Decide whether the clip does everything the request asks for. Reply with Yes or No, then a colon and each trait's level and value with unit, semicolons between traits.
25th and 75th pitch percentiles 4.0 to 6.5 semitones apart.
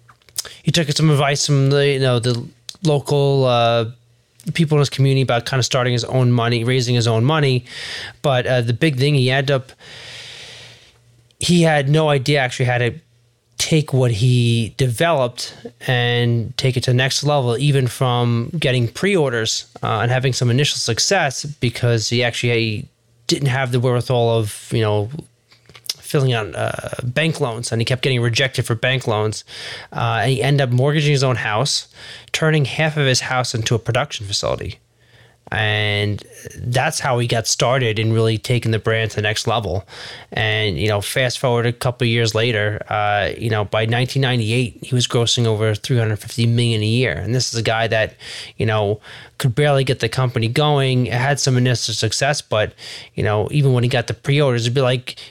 No: average, 2.8 semitones